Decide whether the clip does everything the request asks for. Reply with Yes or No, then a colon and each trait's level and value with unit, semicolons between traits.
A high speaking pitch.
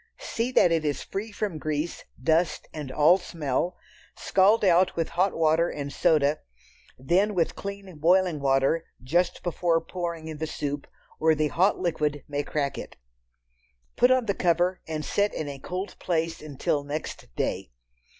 No: medium, 165 Hz